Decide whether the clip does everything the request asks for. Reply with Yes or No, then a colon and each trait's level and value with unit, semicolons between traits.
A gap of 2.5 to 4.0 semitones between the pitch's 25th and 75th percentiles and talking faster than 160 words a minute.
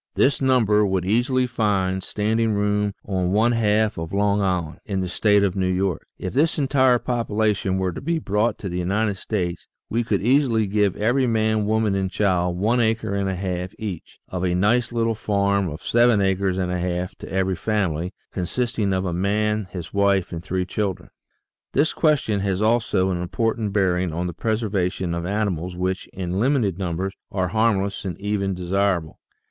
Yes: average, 3.1 semitones; average, 185 wpm